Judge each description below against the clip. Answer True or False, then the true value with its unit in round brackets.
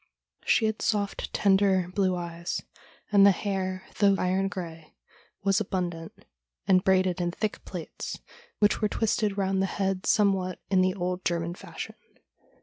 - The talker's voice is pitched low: False (190 Hz)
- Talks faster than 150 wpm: False (145 wpm)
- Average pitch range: False (1.8 semitones)